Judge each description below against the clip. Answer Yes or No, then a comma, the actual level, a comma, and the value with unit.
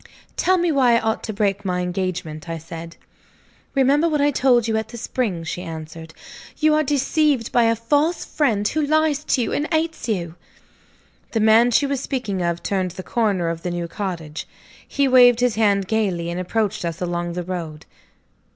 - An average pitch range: No, wide, 7.1 semitones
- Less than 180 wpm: No, average, 190 wpm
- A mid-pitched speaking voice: No, high, 215 Hz